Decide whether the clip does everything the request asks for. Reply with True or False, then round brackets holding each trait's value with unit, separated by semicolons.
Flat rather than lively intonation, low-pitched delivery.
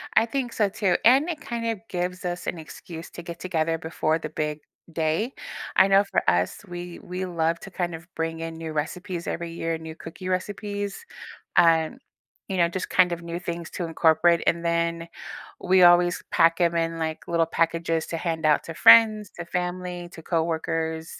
False (1.9 semitones; 170 Hz)